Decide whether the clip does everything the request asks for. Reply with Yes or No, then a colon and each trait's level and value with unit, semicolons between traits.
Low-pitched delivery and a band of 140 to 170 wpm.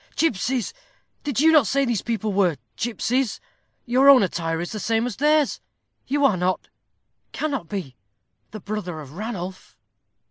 No: high, 225 Hz; average, 150 wpm